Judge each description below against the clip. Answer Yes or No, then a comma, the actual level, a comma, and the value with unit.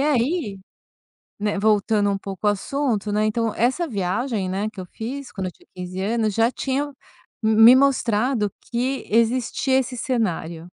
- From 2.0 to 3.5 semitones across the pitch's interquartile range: No, average, 4.1 semitones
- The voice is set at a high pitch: Yes, high, 220 Hz